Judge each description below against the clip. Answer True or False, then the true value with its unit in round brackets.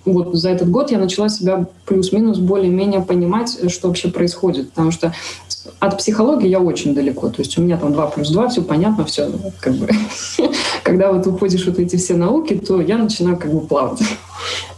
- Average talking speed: False (190 wpm)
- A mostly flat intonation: True (2.3 semitones)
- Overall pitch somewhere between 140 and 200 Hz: True (185 Hz)